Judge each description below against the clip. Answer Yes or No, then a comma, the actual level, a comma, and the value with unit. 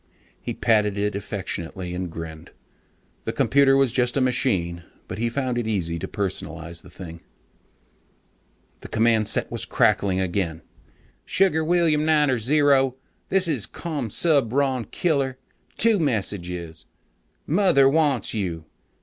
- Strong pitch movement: Yes, wide, 7.5 semitones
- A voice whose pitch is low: Yes, low, 115 Hz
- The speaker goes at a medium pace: No, slow, 125 wpm